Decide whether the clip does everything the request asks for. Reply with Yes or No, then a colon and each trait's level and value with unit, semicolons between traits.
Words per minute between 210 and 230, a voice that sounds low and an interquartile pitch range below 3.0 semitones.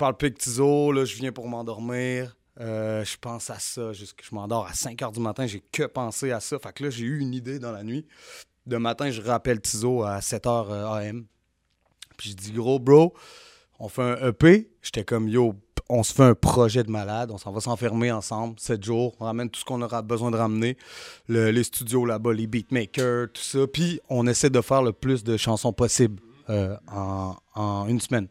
Yes: fast, 220 wpm; low, 120 Hz; narrow, 2.4 semitones